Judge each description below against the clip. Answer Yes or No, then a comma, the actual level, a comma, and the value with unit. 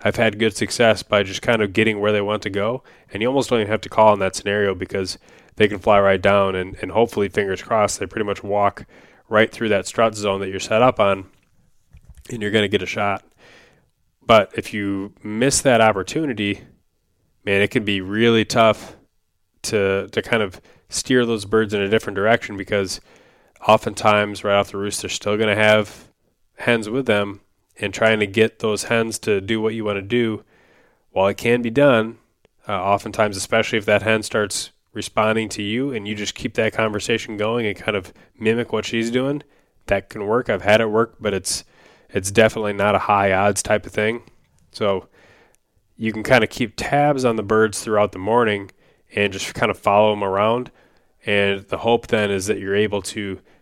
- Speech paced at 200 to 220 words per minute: Yes, fast, 205 wpm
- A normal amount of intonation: No, narrow, 2.0 semitones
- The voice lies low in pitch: Yes, low, 105 Hz